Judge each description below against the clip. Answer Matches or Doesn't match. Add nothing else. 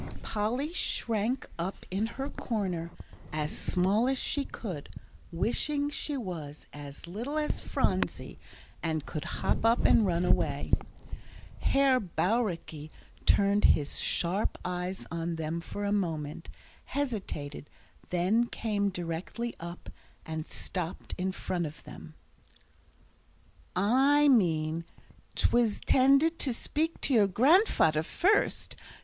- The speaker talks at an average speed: Doesn't match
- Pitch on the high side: Matches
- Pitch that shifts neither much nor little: Doesn't match